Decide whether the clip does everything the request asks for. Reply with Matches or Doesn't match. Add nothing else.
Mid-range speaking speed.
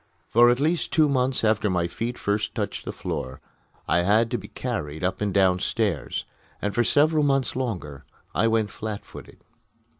Matches